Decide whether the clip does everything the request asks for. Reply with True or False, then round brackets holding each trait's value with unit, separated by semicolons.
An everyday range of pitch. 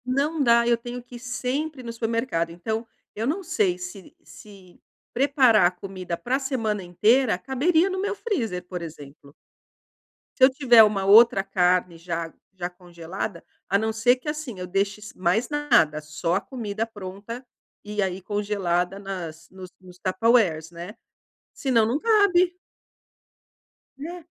False (5.8 semitones)